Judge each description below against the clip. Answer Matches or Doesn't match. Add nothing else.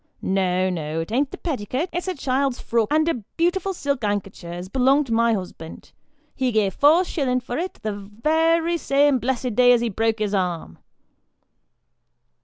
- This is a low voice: Doesn't match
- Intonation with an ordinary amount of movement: Doesn't match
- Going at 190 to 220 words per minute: Doesn't match